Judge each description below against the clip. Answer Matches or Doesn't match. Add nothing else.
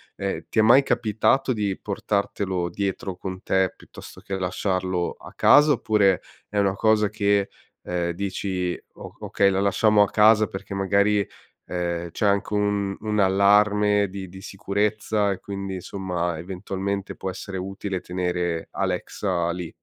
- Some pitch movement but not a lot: Doesn't match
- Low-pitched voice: Matches